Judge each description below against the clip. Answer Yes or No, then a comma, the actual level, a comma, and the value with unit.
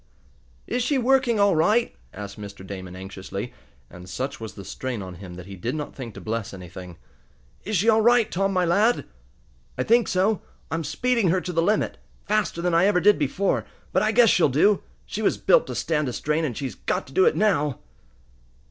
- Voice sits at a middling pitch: Yes, medium, 165 Hz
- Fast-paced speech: Yes, fast, 210 wpm